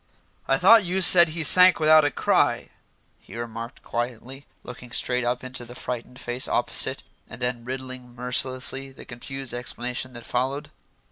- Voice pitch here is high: No, low, 125 Hz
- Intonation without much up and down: Yes, narrow, 1.9 semitones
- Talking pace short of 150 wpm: No, average, 155 wpm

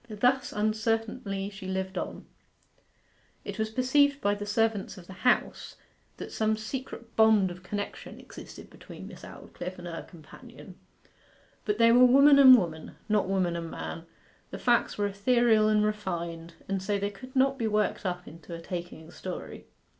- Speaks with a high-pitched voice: Yes, high, 205 Hz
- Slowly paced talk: No, average, 165 wpm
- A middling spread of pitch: Yes, average, 3.9 semitones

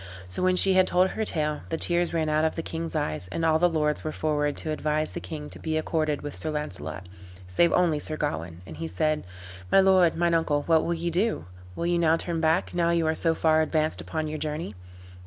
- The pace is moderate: No, fast, 235 wpm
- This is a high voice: No, medium, 160 Hz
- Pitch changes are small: Yes, narrow, 2.1 semitones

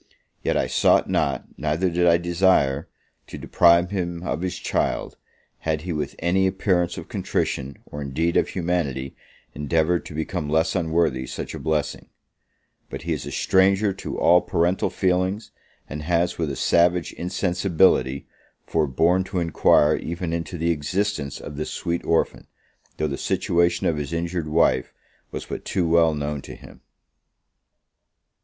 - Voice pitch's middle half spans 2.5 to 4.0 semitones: Yes, average, 2.8 semitones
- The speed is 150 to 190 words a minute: Yes, average, 155 wpm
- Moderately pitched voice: No, very low, 85 Hz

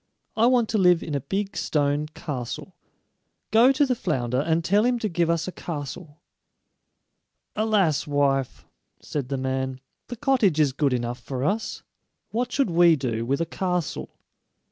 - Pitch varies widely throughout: Yes, wide, 7.1 semitones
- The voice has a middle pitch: Yes, medium, 165 Hz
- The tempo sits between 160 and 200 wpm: Yes, average, 165 wpm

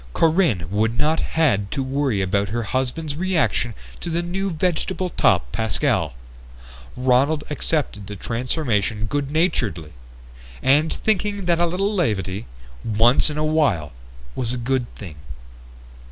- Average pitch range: No, wide, 7.1 semitones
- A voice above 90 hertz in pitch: Yes, low, 135 Hz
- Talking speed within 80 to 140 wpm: Yes, slow, 135 wpm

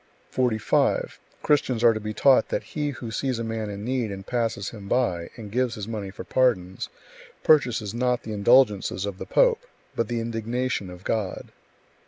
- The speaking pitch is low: Yes, low, 115 Hz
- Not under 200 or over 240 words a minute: No, average, 185 wpm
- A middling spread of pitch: Yes, average, 3.6 semitones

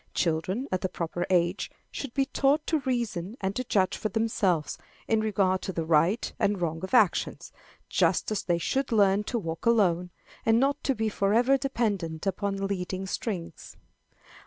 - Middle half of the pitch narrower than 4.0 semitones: No, average, 4.6 semitones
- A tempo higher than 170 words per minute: No, average, 165 wpm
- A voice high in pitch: Yes, high, 195 Hz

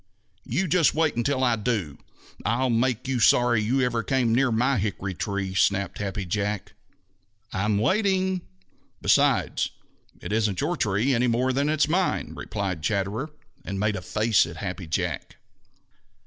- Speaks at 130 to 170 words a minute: Yes, average, 150 wpm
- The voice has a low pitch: Yes, low, 115 Hz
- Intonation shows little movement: No, average, 4.7 semitones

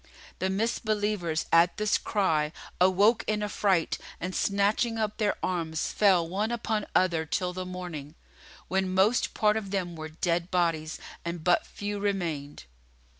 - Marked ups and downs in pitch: No, average, 3.5 semitones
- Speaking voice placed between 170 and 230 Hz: Yes, medium, 185 Hz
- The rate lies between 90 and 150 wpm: Yes, average, 145 wpm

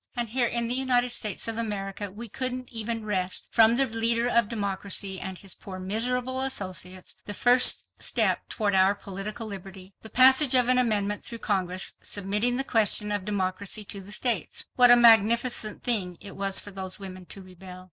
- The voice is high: Yes, high, 210 Hz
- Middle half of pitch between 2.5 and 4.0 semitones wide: Yes, average, 3.6 semitones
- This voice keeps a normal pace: Yes, average, 180 wpm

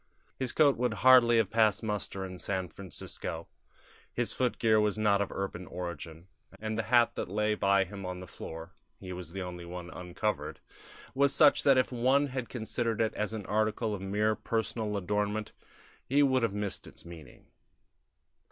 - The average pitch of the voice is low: Yes, low, 105 Hz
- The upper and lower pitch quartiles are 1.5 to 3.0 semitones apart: No, average, 4.1 semitones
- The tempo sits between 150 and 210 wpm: Yes, average, 175 wpm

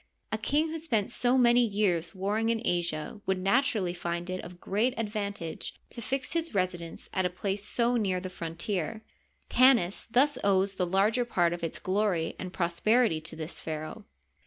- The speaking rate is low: No, average, 185 wpm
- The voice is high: Yes, high, 195 Hz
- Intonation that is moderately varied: Yes, average, 4.7 semitones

